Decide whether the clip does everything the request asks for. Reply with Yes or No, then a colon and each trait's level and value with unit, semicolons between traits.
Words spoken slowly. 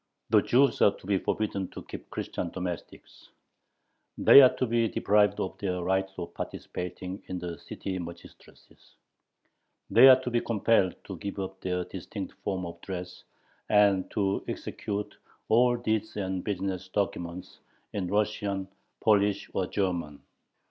No: average, 145 wpm